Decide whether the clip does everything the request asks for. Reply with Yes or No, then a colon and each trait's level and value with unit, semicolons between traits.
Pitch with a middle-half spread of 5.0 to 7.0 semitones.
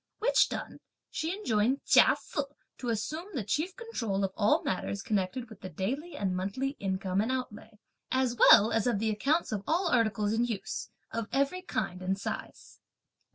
Yes: wide, 5.6 semitones